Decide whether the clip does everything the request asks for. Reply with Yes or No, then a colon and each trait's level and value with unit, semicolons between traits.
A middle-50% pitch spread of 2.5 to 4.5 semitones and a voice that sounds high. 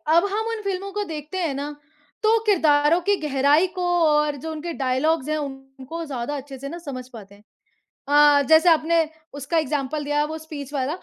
Yes: average, 3.1 semitones; very high, 300 Hz